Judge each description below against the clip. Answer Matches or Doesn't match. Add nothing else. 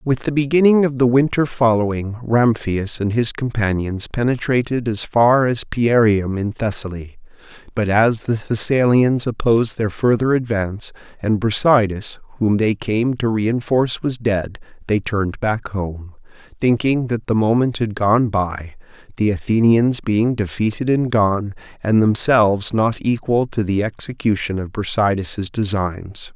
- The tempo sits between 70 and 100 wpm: Doesn't match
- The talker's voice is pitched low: Matches